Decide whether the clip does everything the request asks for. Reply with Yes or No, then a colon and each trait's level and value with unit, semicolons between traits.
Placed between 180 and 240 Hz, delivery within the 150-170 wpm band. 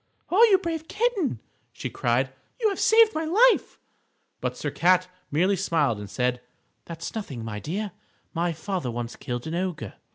Yes: medium, 185 Hz; average, 165 wpm